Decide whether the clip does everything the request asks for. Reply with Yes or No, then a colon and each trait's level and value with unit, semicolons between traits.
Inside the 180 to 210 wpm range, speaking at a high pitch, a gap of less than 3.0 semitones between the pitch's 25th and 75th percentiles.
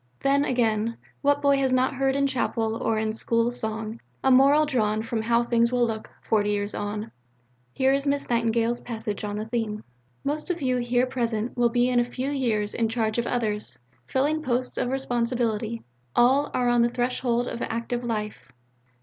Yes: average, 185 wpm; high, 240 Hz; narrow, 2.6 semitones